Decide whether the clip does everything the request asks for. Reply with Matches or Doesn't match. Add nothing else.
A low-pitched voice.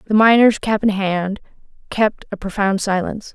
Doesn't match